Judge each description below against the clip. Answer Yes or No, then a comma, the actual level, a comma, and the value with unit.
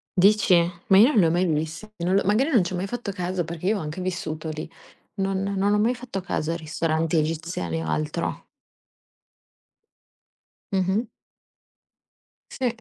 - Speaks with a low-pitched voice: No, medium, 185 Hz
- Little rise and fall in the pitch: No, average, 3.9 semitones